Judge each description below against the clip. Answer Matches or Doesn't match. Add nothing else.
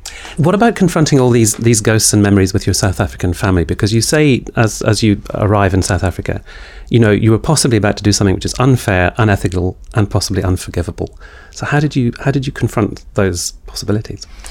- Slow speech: Doesn't match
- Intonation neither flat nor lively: Matches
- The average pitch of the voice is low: Matches